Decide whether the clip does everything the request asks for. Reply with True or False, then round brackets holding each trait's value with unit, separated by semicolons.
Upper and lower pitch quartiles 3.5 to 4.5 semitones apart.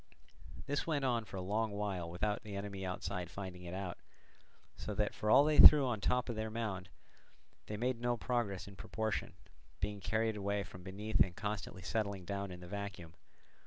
False (2.8 semitones)